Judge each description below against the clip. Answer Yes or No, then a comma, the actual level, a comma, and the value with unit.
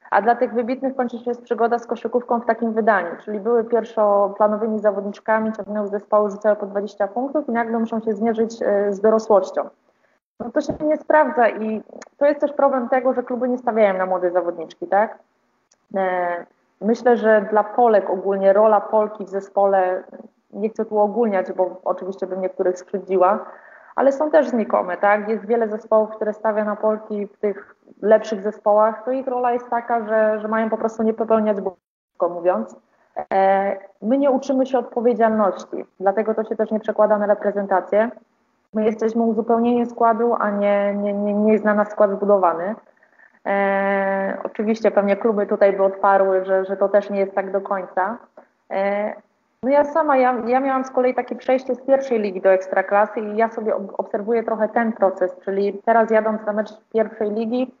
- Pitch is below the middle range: No, high, 215 Hz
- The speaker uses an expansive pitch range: No, average, 2.8 semitones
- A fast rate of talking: Yes, fast, 180 wpm